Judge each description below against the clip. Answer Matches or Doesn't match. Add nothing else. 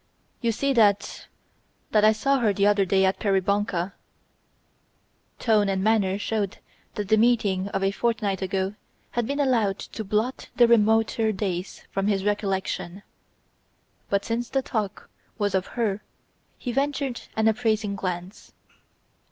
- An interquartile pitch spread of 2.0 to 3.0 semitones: Matches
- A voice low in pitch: Doesn't match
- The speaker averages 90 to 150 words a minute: Matches